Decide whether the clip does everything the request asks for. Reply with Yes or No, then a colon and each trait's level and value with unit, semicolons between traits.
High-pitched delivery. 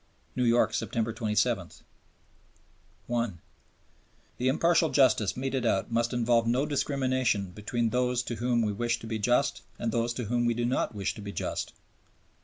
No: low, 120 Hz